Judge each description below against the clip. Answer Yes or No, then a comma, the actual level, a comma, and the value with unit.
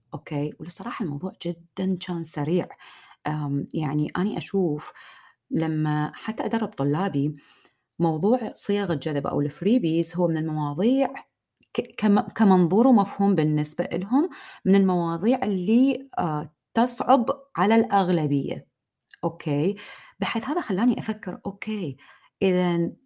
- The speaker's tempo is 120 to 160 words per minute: No, average, 95 wpm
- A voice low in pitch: No, medium, 185 Hz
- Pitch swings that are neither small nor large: No, wide, 5.7 semitones